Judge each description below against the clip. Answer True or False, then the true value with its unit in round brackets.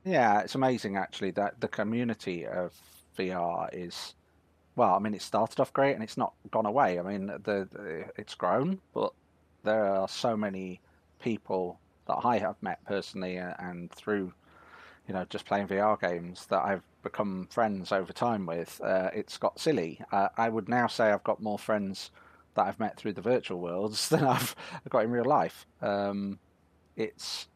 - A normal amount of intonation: True (3.5 semitones)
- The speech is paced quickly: False (180 wpm)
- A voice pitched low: True (100 Hz)